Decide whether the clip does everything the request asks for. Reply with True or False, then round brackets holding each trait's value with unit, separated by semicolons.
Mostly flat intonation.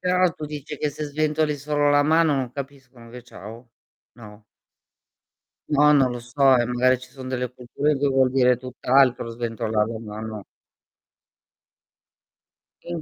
False (3.3 semitones)